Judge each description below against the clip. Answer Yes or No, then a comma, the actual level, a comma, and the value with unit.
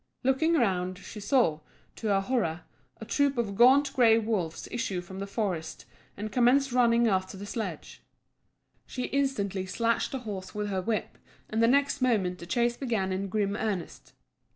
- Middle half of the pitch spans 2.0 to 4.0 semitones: No, average, 4.5 semitones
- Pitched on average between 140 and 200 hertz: No, high, 215 Hz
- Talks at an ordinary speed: Yes, average, 170 wpm